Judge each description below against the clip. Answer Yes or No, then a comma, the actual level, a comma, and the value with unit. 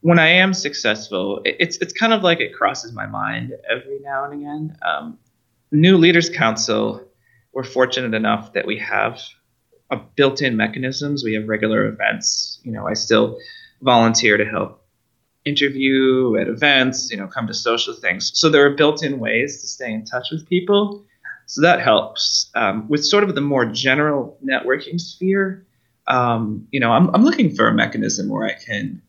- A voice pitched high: No, medium, 140 Hz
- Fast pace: No, average, 175 wpm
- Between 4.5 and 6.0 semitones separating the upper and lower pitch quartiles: Yes, wide, 5.6 semitones